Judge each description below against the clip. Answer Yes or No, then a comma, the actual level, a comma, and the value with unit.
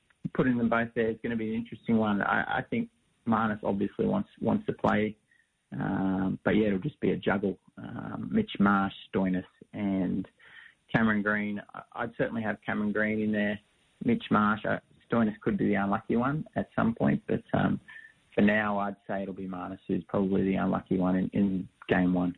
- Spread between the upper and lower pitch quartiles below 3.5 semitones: Yes, average, 2.8 semitones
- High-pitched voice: No, low, 105 Hz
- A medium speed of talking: Yes, average, 195 wpm